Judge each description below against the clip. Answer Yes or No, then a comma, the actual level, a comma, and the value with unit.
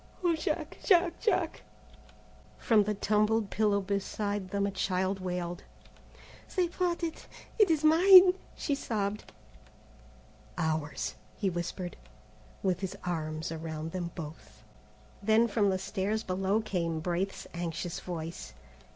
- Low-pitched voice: No, high, 195 Hz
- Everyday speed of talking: No, slow, 125 wpm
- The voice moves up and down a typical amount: Yes, average, 4.3 semitones